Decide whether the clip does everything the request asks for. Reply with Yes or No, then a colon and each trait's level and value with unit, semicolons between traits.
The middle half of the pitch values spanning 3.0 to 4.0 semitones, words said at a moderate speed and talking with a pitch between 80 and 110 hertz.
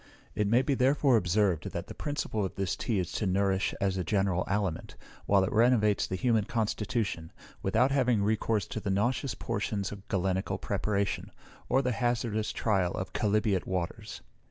Yes: average, 3.4 semitones; average, 170 wpm; low, 105 Hz